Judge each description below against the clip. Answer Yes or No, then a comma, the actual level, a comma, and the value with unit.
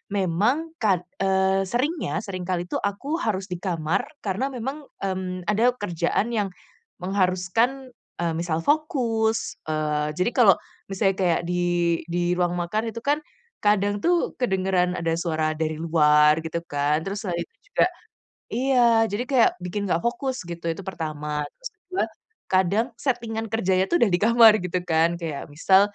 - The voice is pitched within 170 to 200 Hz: Yes, high, 190 Hz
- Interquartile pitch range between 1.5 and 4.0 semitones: No, average, 4.7 semitones